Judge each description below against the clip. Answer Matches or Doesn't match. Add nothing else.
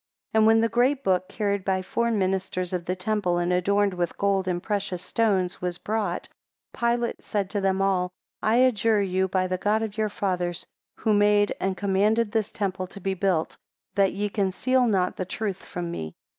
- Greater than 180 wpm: Matches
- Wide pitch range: Doesn't match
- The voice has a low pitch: Doesn't match